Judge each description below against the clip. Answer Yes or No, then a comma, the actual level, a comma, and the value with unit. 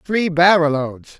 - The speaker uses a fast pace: No, average, 150 wpm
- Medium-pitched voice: Yes, medium, 165 Hz